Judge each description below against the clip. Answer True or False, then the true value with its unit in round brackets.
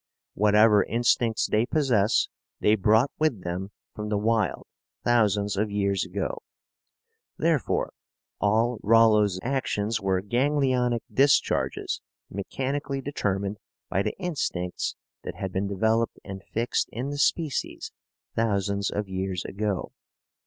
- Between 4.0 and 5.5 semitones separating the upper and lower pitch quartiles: False (3.6 semitones)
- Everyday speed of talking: False (115 wpm)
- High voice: False (105 Hz)